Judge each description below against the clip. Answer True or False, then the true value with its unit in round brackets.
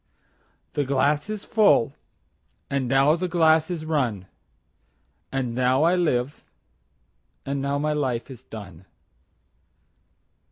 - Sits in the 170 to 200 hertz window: False (140 Hz)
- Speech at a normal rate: False (110 wpm)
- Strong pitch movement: False (4.3 semitones)